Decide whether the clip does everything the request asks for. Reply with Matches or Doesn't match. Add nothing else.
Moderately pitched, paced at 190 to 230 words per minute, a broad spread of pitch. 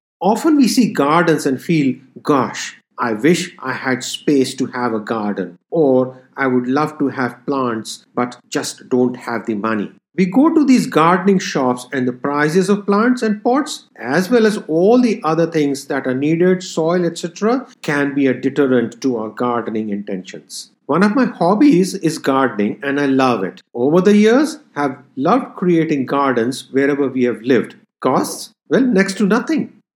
Doesn't match